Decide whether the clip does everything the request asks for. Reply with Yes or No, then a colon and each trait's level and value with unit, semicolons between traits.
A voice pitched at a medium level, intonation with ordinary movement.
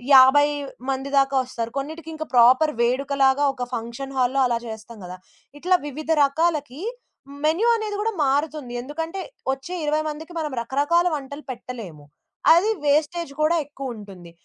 No: very high, 280 Hz; average, 3.8 semitones